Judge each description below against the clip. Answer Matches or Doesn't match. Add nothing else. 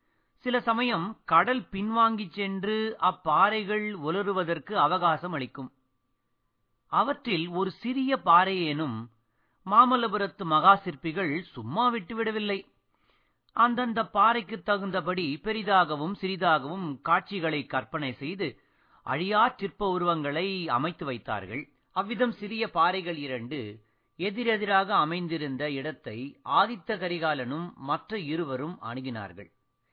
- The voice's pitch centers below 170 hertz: Doesn't match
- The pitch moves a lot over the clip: Matches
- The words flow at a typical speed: Matches